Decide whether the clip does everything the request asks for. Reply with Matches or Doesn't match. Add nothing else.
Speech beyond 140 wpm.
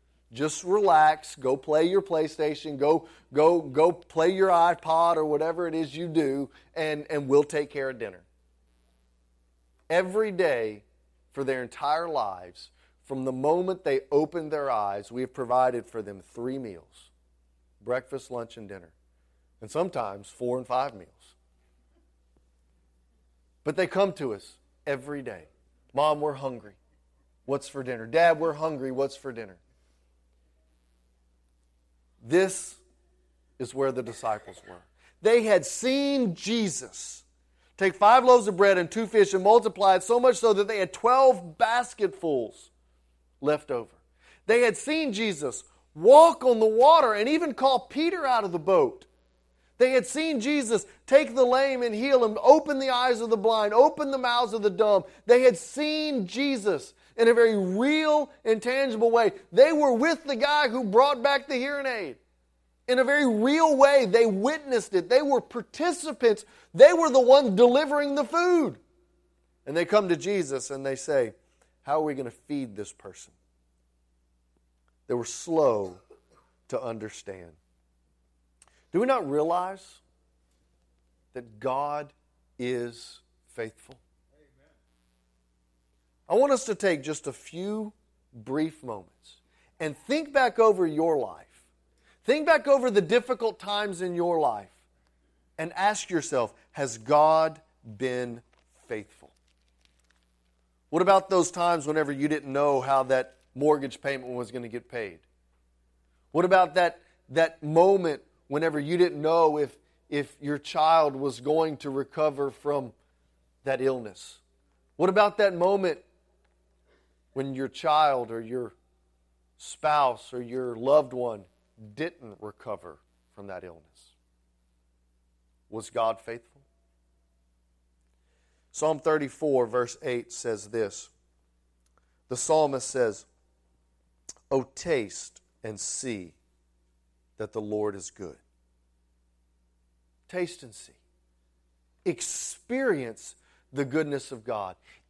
Doesn't match